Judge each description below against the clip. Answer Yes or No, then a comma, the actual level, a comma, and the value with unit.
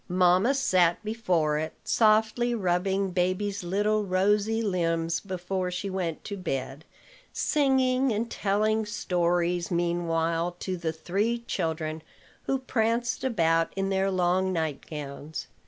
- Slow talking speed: Yes, slow, 120 wpm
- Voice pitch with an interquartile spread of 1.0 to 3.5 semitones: No, average, 4.0 semitones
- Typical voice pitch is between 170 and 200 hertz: Yes, medium, 185 Hz